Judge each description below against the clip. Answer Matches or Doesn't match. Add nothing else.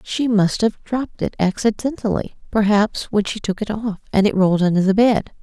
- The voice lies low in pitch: Doesn't match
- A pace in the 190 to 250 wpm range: Matches